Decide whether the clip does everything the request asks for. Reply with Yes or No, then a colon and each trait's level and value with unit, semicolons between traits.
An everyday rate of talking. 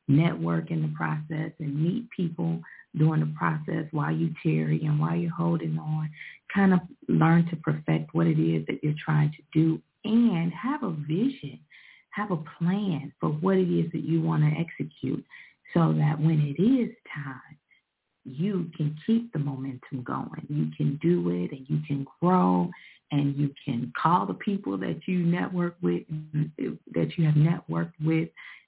Yes: average, 170 wpm